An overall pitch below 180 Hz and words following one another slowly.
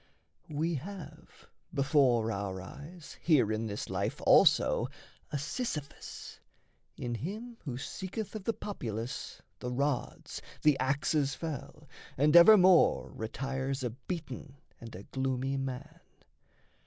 Yes: medium, 140 Hz; slow, 115 wpm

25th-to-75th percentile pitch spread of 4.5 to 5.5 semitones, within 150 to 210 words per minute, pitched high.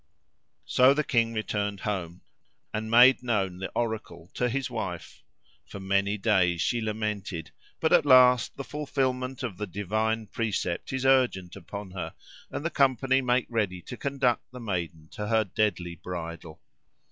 No: average, 5.1 semitones; average, 155 wpm; low, 110 Hz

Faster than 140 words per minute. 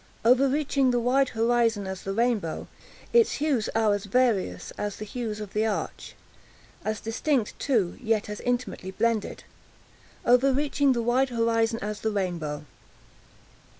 No: slow, 135 wpm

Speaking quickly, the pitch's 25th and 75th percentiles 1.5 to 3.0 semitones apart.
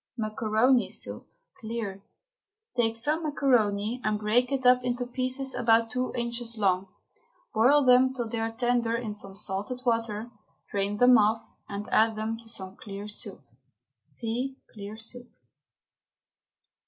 No: average, 140 wpm; average, 2.7 semitones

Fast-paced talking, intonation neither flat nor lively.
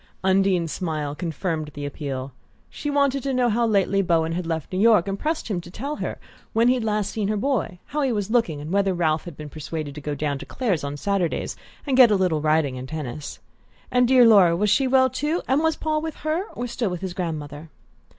No: fast, 230 wpm; wide, 7.8 semitones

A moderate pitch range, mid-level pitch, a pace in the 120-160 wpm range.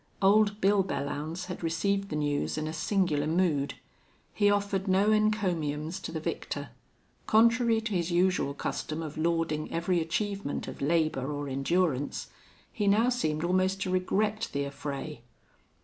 Yes: average, 4.7 semitones; medium, 175 Hz; average, 150 wpm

